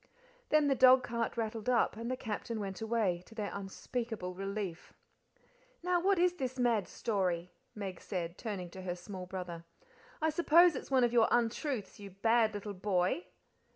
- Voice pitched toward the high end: Yes, high, 220 Hz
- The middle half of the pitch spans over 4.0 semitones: Yes, average, 4.8 semitones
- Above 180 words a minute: No, average, 165 wpm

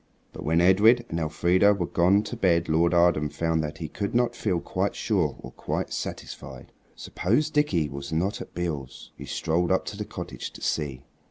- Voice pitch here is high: No, very low, 85 Hz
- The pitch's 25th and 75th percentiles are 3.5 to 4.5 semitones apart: Yes, average, 4.1 semitones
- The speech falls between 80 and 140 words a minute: No, average, 190 wpm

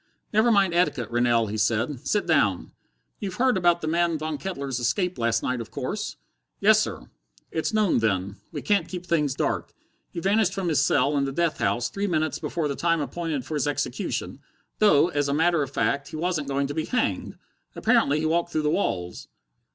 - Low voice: No, medium, 155 Hz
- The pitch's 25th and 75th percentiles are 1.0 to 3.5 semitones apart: No, average, 4.6 semitones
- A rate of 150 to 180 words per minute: No, average, 200 wpm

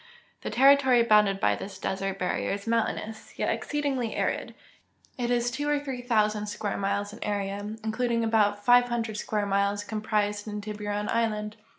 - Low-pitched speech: No, high, 215 Hz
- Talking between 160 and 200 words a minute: Yes, average, 165 wpm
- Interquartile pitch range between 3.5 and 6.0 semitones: No, narrow, 2.5 semitones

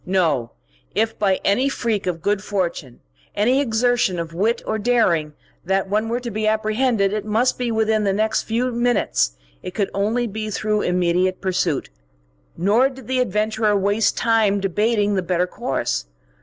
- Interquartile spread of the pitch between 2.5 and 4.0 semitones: Yes, average, 3.3 semitones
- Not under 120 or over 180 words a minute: Yes, average, 165 wpm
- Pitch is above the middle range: Yes, high, 210 Hz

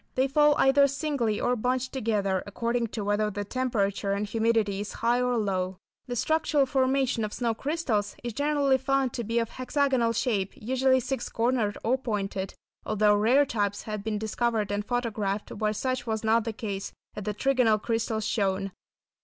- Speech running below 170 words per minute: No, average, 175 wpm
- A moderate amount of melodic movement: Yes, average, 3.8 semitones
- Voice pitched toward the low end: No, high, 230 Hz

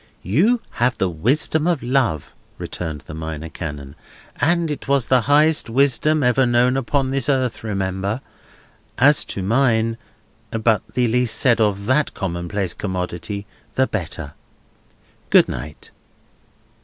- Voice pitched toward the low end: Yes, low, 115 Hz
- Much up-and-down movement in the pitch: Yes, wide, 6.2 semitones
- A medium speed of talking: No, slow, 130 wpm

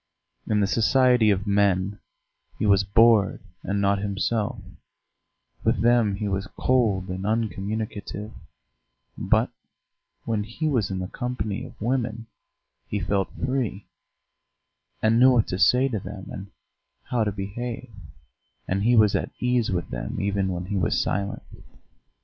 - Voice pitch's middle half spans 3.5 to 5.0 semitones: No, average, 3.0 semitones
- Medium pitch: No, low, 105 Hz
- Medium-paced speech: Yes, average, 145 wpm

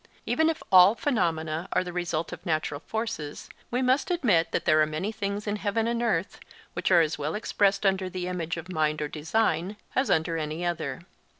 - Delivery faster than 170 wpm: Yes, average, 200 wpm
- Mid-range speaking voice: Yes, medium, 180 Hz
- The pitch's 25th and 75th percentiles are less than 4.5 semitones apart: No, average, 5.1 semitones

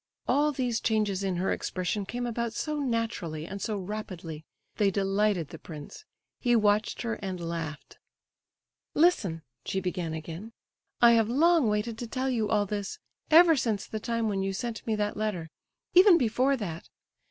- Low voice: No, high, 210 Hz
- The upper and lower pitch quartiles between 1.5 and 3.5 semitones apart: No, average, 4.1 semitones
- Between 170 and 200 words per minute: No, average, 160 wpm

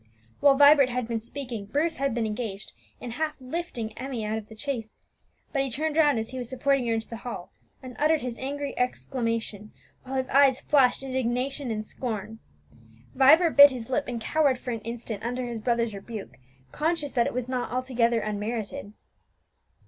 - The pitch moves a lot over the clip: No, average, 3.4 semitones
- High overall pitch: Yes, very high, 250 Hz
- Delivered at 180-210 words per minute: Yes, average, 185 wpm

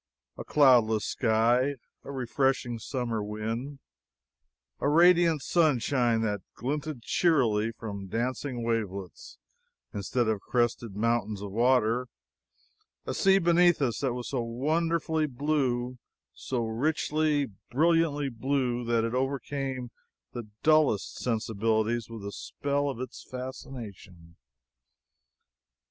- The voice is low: Yes, low, 125 Hz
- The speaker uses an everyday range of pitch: Yes, average, 4.1 semitones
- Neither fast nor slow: No, slow, 110 wpm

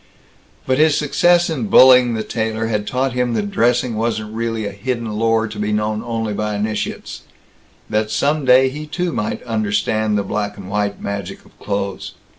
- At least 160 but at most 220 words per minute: Yes, average, 180 wpm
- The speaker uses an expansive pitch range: No, average, 3.2 semitones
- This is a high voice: No, low, 110 Hz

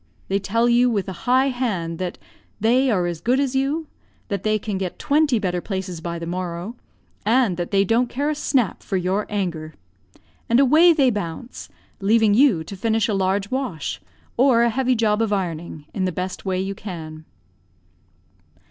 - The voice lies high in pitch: Yes, high, 205 Hz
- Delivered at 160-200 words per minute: Yes, average, 185 wpm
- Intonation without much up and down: No, average, 5.2 semitones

